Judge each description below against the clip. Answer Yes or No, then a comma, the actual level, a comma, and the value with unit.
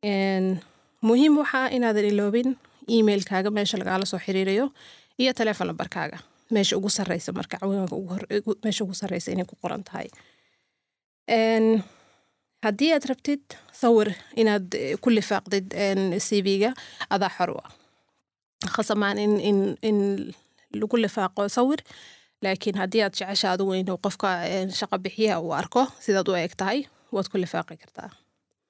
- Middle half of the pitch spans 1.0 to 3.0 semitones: Yes, average, 2.7 semitones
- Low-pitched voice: No, high, 205 Hz